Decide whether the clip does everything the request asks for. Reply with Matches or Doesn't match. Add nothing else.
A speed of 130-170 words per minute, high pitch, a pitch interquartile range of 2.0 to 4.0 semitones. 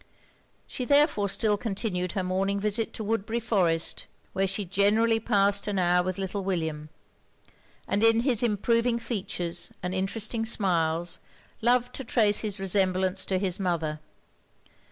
Matches